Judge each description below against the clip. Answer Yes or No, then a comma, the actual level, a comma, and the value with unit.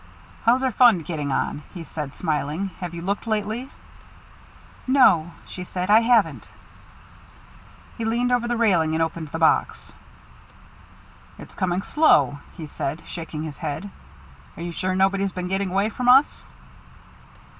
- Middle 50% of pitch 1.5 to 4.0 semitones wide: No, wide, 5.6 semitones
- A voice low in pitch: No, medium, 185 Hz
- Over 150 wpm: No, average, 145 wpm